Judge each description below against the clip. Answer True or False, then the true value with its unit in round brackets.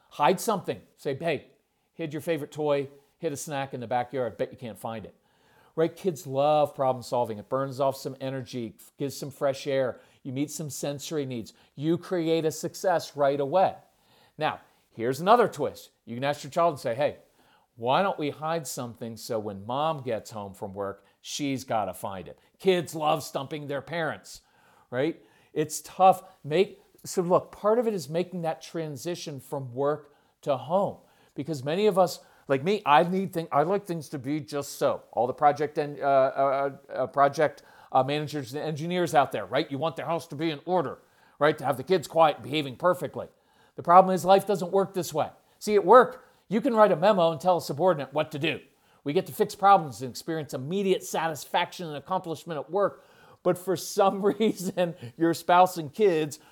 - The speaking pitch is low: False (155 Hz)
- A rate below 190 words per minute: False (200 wpm)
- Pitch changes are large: False (4.4 semitones)